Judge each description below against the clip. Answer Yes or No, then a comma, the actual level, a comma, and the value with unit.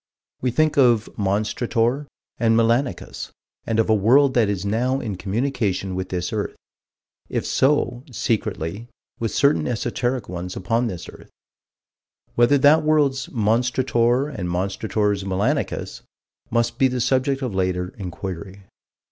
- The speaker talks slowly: Yes, slow, 130 wpm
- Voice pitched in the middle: No, low, 115 Hz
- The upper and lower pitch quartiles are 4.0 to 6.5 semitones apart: Yes, average, 4.7 semitones